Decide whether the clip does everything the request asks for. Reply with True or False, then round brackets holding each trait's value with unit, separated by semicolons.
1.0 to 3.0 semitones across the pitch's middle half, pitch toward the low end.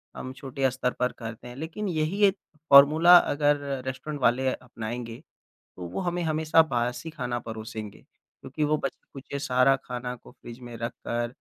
False (4.1 semitones; 130 Hz)